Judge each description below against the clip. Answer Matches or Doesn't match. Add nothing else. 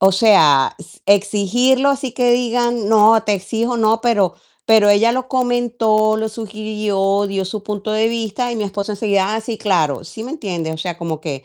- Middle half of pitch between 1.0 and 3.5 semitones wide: Matches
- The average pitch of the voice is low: Doesn't match